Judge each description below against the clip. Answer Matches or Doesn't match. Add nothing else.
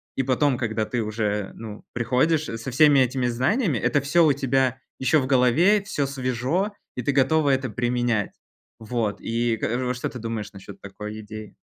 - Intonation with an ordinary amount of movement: Matches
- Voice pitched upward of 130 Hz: Doesn't match